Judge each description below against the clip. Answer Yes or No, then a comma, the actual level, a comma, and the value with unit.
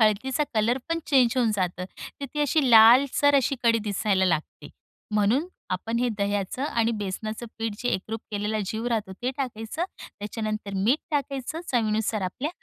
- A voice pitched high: Yes, high, 225 Hz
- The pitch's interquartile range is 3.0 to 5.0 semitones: Yes, average, 3.8 semitones